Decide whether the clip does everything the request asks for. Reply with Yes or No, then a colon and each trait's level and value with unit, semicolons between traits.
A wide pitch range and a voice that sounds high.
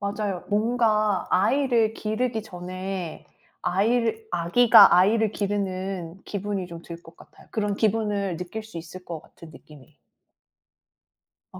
No: average, 3.5 semitones; high, 200 Hz